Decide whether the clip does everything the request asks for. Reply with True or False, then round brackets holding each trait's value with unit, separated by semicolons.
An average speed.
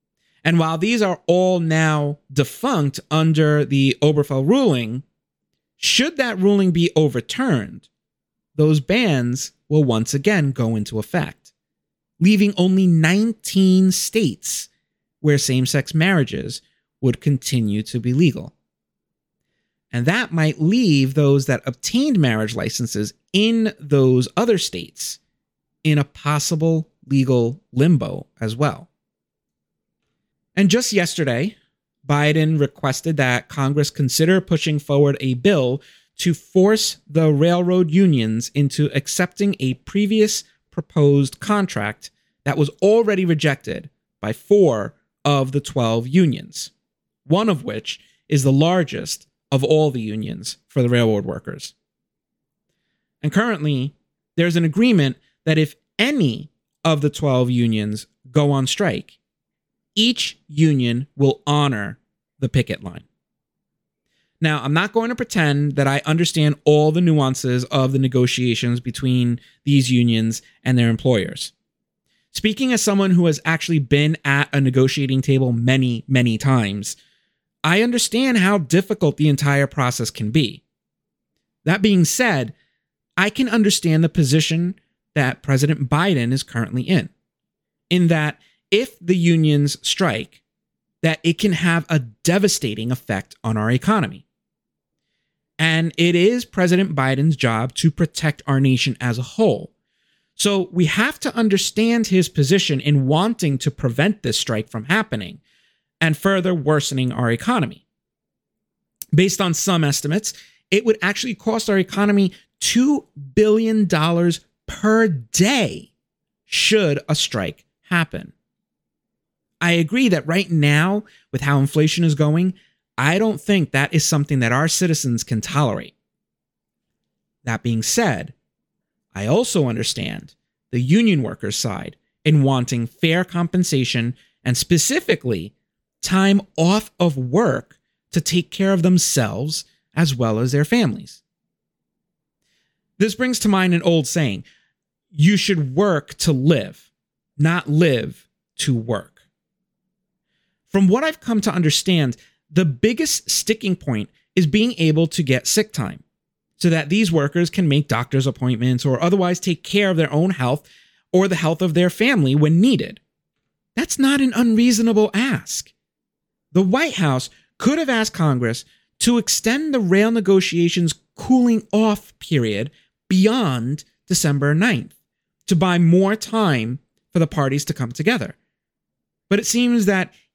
False (130 wpm)